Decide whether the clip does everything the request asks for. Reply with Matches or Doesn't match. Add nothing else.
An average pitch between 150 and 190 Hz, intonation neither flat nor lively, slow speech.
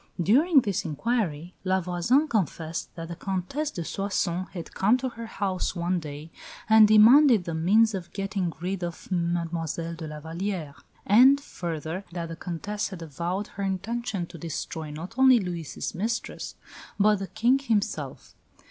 Doesn't match